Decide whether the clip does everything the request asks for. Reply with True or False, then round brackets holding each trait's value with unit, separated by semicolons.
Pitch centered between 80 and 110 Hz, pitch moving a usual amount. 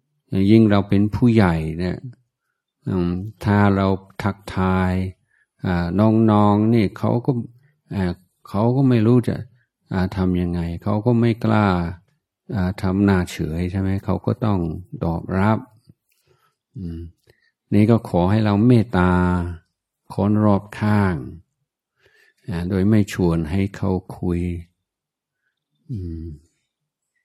True (100 Hz; 3.7 semitones)